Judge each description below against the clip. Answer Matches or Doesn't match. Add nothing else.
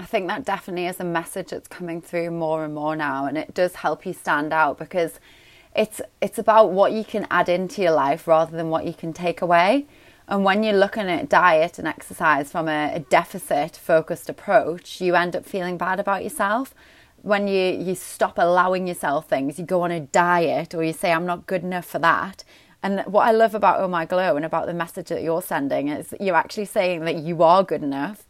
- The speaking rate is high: Matches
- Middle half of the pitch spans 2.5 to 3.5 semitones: Matches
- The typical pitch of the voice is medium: Matches